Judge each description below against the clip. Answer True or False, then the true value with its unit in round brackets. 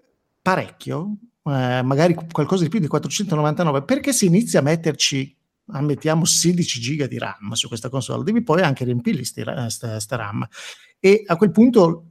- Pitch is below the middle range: False (155 Hz)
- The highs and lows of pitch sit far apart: True (6.1 semitones)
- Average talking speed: True (155 wpm)